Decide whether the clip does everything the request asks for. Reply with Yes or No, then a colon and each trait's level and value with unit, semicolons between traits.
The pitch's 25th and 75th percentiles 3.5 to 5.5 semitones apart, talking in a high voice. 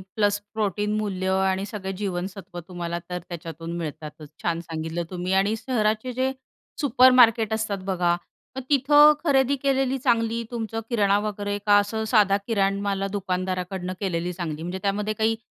Yes: average, 3.8 semitones; high, 200 Hz